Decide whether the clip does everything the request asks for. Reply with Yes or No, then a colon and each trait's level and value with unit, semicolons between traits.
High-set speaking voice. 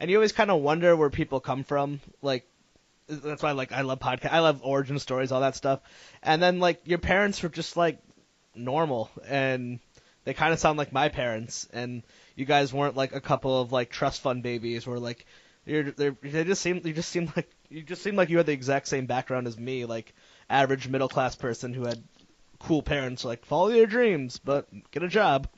No: medium, 140 Hz